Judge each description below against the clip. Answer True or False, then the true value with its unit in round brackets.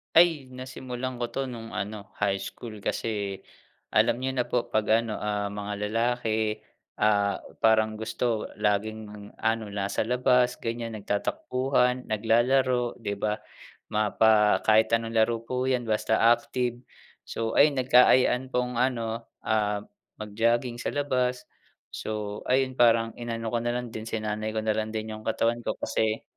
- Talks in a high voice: False (115 Hz)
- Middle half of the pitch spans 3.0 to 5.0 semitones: False (2.5 semitones)